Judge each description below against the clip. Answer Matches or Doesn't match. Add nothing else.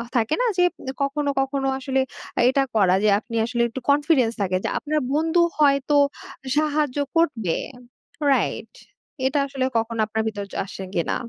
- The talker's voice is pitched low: Doesn't match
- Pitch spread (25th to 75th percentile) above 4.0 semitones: Matches